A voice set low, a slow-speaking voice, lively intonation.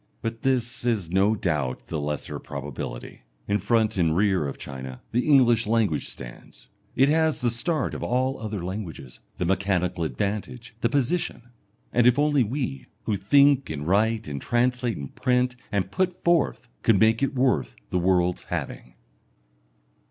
No: low, 110 Hz; average, 160 wpm; wide, 6.0 semitones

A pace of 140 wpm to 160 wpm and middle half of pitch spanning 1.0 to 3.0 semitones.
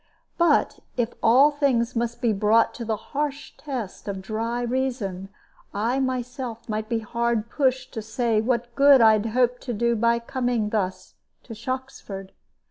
Yes: average, 155 wpm; average, 2.7 semitones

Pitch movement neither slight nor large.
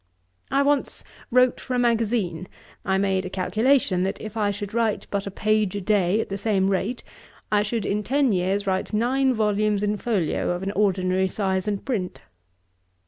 Yes: average, 3.0 semitones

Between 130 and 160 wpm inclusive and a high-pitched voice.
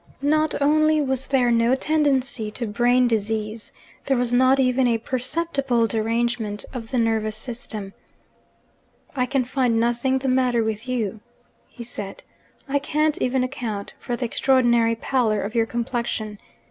Yes: average, 145 wpm; high, 245 Hz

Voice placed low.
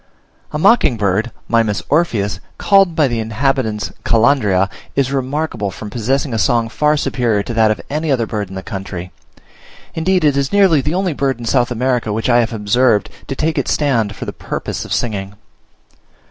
Yes: low, 120 Hz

